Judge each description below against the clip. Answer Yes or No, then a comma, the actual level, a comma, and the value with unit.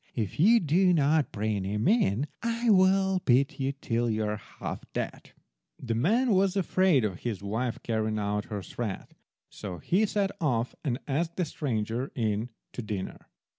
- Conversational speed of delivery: Yes, average, 170 wpm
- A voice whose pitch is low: Yes, low, 130 Hz